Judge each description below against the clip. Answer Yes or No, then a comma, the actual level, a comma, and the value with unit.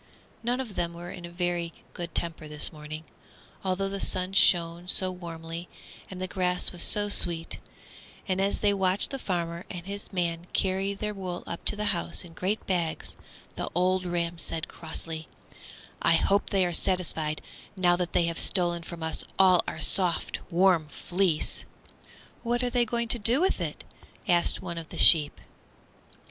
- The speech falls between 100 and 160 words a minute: No, average, 175 wpm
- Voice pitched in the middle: Yes, medium, 180 Hz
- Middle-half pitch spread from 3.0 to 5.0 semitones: No, narrow, 2.4 semitones